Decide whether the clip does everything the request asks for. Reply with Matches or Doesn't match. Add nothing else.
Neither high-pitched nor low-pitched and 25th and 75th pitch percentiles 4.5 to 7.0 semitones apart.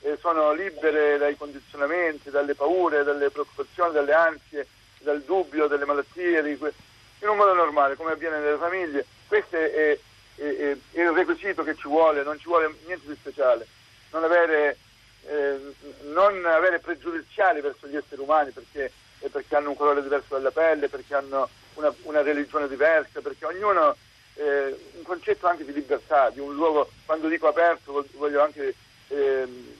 Doesn't match